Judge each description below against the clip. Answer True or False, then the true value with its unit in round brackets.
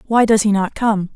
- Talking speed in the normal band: False (260 wpm)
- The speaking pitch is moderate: False (210 Hz)